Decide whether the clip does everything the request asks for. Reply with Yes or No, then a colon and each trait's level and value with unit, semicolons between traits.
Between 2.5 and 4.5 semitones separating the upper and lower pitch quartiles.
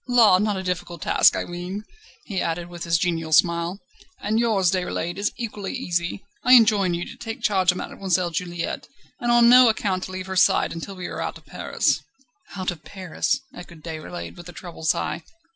Yes: average, 3.0 semitones